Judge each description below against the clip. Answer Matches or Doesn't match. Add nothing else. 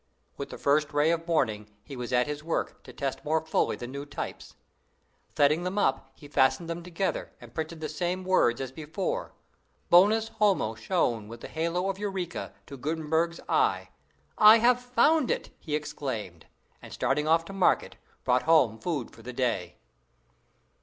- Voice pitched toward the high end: Doesn't match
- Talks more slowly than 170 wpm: Doesn't match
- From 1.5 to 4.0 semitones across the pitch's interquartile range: Doesn't match